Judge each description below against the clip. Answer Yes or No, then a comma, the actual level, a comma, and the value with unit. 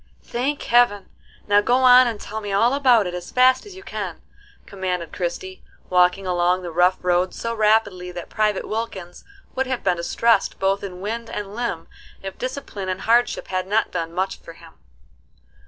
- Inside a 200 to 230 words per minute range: No, average, 180 wpm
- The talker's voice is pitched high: Yes, high, 200 Hz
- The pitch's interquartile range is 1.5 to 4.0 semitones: No, average, 4.4 semitones